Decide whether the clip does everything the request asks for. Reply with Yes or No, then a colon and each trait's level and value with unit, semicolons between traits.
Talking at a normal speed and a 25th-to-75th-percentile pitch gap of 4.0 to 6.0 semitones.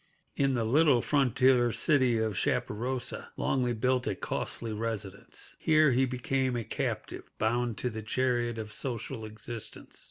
No: average, 145 wpm; average, 2.7 semitones